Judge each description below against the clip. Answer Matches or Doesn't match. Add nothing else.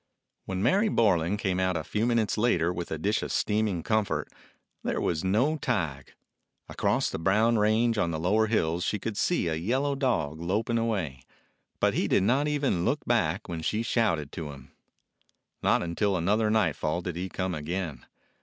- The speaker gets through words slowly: Doesn't match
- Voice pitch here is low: Matches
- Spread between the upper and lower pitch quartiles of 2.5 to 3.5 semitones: Doesn't match